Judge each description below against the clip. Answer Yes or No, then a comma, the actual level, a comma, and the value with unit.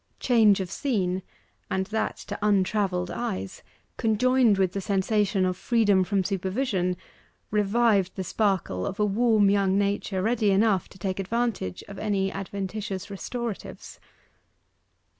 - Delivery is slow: Yes, slow, 130 wpm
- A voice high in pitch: Yes, high, 200 Hz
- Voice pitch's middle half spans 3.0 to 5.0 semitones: No, narrow, 2.4 semitones